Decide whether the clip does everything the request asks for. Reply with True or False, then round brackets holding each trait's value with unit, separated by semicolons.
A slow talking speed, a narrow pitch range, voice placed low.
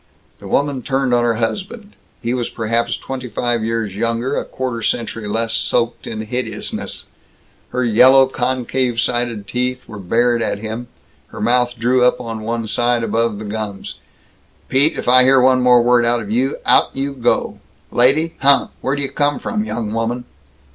False (175 wpm; 2.1 semitones; 120 Hz)